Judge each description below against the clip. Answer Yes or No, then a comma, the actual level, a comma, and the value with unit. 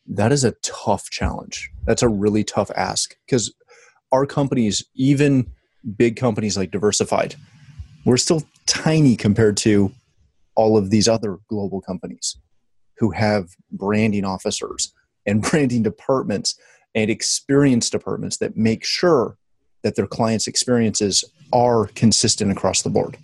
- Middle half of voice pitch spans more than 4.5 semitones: No, average, 3.2 semitones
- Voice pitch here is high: No, low, 110 Hz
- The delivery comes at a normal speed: No, slow, 130 wpm